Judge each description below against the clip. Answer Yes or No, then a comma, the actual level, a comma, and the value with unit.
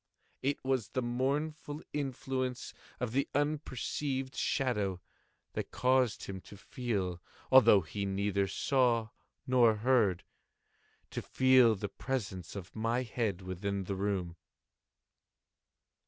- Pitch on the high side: No, low, 115 Hz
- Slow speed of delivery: Yes, slow, 110 wpm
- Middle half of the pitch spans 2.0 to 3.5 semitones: No, average, 4.8 semitones